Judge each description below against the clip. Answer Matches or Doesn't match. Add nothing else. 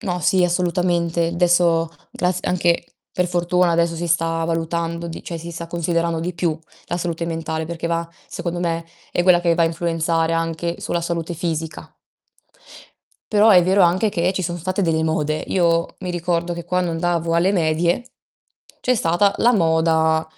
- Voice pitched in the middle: Matches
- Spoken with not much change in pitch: Matches